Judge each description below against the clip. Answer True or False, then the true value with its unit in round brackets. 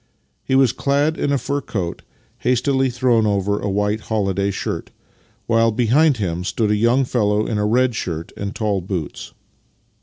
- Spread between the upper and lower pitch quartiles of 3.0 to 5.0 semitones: True (4.1 semitones)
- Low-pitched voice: True (110 Hz)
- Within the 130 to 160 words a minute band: False (170 wpm)